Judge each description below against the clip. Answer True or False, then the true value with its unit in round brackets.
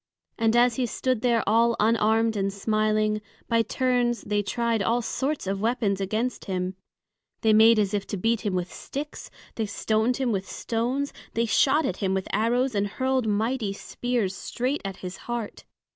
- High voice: True (225 Hz)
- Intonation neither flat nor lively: True (3.0 semitones)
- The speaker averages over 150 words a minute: True (175 wpm)